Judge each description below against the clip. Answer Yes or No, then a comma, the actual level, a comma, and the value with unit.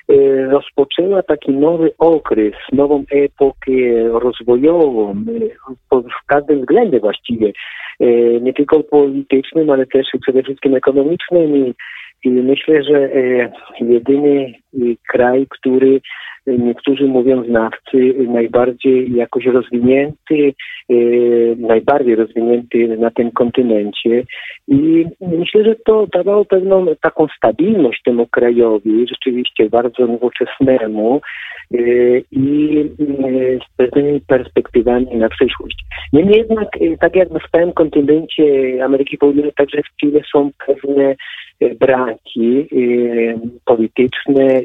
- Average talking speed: No, slow, 100 wpm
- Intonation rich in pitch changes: No, average, 3.5 semitones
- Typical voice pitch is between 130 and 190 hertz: Yes, low, 135 Hz